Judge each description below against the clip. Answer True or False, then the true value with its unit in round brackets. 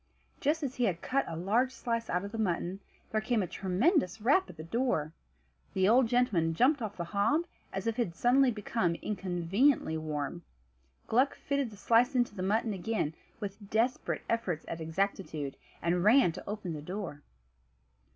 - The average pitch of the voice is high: True (205 Hz)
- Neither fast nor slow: True (180 wpm)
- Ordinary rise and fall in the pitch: False (5.8 semitones)